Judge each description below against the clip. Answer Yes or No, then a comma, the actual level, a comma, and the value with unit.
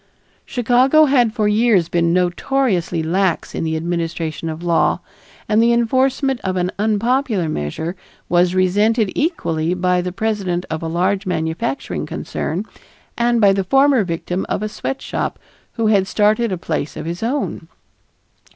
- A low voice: No, high, 195 Hz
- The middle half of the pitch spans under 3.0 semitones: No, average, 5.3 semitones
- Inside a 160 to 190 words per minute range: No, average, 150 wpm